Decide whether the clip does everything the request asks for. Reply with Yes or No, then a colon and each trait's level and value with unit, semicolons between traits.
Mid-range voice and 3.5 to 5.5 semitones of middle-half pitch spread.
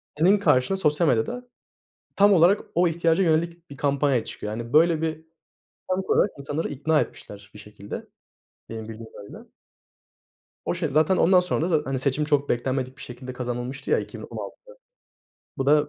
Yes: medium, 150 Hz; average, 5.0 semitones